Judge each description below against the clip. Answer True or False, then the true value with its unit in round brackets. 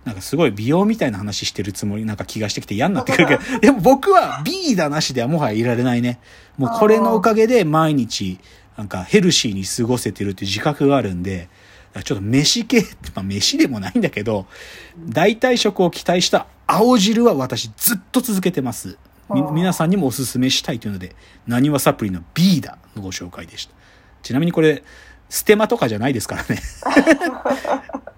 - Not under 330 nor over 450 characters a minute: True (390 characters per minute)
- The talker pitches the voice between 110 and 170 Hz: True (135 Hz)